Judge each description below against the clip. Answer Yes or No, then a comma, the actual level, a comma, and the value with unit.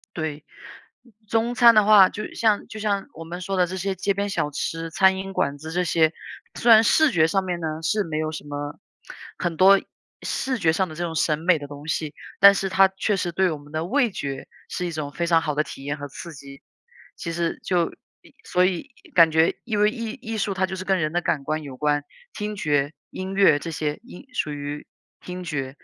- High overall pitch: No, medium, 170 Hz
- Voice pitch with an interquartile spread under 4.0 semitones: No, average, 4.3 semitones